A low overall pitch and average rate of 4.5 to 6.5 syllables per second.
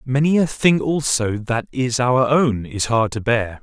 No: low, 125 Hz; 4.0 syllables/s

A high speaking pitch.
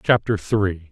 No: low, 100 Hz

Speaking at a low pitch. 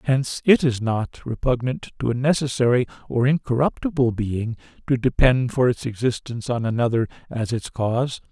Yes: low, 125 Hz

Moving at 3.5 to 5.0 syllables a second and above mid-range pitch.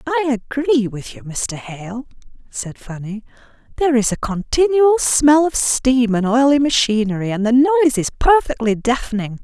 Yes: 4.7 syllables/s; high, 245 Hz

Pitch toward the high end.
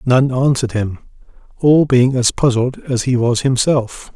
No: low, 125 Hz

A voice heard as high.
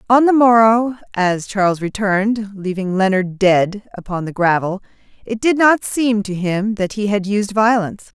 Yes: high, 205 Hz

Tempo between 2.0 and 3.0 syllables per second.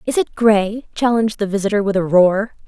No: 5.5 syllables/s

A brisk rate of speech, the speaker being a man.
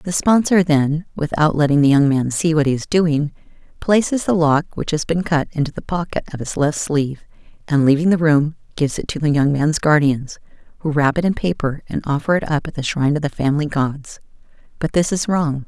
No: fast, 220 wpm; female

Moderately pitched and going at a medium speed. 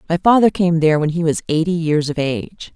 No: medium, 165 Hz; fast, 240 wpm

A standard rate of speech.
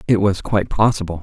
Yes: average, 195 wpm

